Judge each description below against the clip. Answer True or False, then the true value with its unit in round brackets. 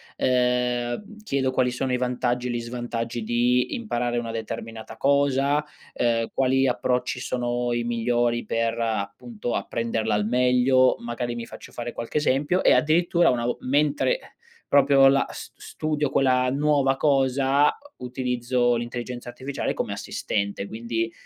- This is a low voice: True (125 Hz)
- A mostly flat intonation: True (2.3 semitones)